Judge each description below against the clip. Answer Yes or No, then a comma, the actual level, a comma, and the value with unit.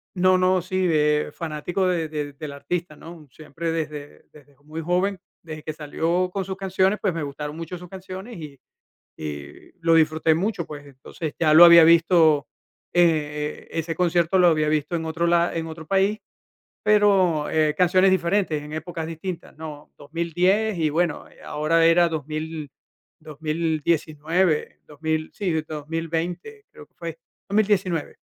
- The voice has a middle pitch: Yes, medium, 165 Hz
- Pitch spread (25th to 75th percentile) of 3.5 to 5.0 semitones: No, average, 2.8 semitones